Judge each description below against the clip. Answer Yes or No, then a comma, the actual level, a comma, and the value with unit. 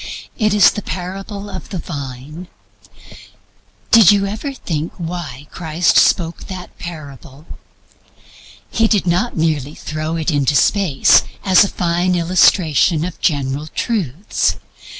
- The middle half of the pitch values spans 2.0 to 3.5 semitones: No, average, 4.0 semitones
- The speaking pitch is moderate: Yes, medium, 170 Hz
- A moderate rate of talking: No, slow, 125 wpm